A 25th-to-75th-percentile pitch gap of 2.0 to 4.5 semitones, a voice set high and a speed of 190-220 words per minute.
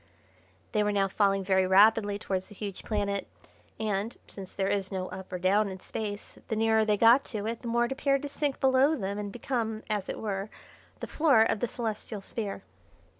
Yes: average, 2.7 semitones; high, 210 Hz; fast, 205 wpm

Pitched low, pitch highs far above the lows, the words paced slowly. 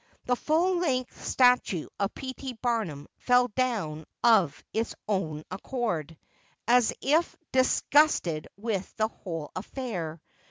No: high, 225 Hz; wide, 7.0 semitones; slow, 120 wpm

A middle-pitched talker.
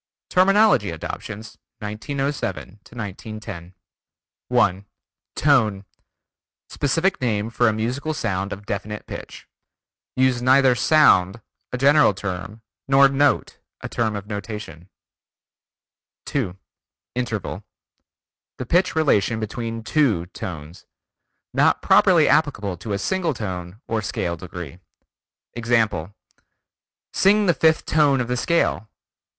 No: low, 110 Hz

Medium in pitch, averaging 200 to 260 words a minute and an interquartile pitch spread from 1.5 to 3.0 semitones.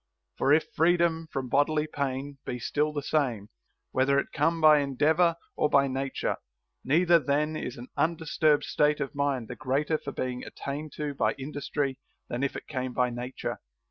No: medium, 145 Hz; average, 175 wpm; narrow, 2.6 semitones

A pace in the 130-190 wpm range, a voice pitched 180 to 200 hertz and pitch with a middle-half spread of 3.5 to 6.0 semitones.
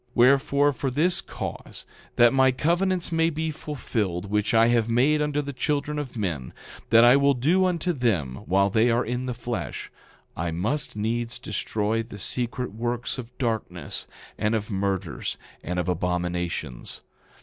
No: average, 160 wpm; low, 120 Hz; wide, 5.4 semitones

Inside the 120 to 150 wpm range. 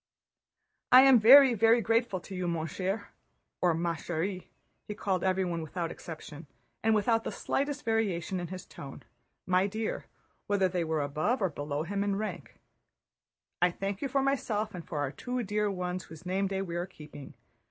No: average, 175 wpm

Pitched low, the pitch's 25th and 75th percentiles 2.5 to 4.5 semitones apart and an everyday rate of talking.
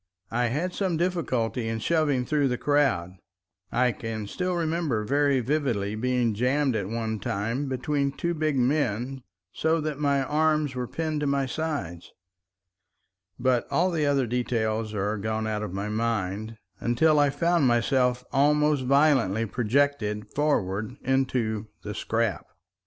No: low, 125 Hz; average, 5.0 semitones; average, 145 wpm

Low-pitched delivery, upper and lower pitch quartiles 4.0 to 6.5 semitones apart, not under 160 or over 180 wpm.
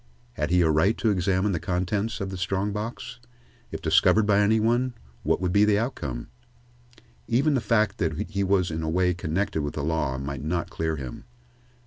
No: very low, 95 Hz; average, 4.8 semitones; average, 195 wpm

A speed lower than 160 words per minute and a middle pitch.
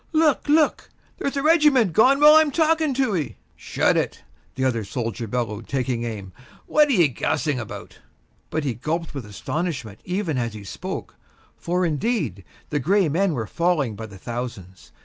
No: average, 170 wpm; medium, 150 Hz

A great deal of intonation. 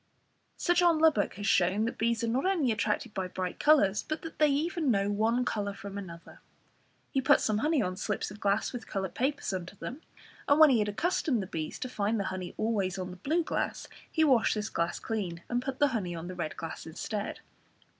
Yes: wide, 6.1 semitones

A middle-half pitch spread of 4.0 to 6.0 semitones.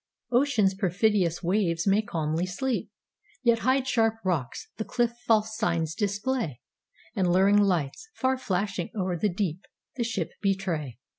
Yes: average, 4.4 semitones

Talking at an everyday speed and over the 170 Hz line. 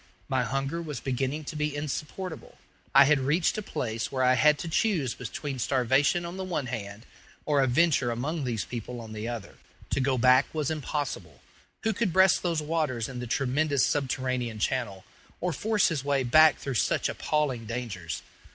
No: average, 180 wpm; low, 135 Hz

